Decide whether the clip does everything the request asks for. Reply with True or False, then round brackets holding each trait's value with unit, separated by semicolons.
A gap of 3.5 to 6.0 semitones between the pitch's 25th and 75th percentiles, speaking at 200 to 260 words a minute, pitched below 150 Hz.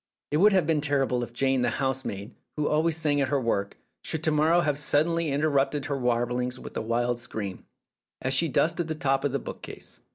True (3.9 semitones; 205 wpm; 140 Hz)